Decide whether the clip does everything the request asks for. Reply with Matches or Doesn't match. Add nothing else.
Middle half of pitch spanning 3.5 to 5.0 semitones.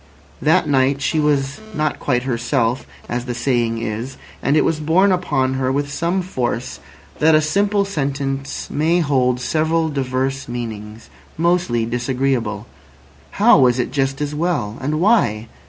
Matches